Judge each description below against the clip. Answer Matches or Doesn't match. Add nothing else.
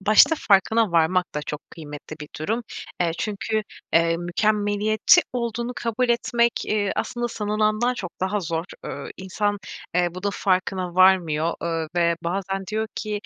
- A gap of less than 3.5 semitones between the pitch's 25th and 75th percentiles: Doesn't match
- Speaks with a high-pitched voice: Matches